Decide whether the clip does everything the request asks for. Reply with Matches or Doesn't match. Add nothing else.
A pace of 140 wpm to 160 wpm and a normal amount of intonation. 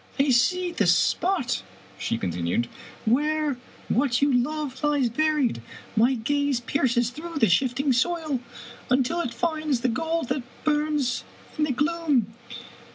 Matches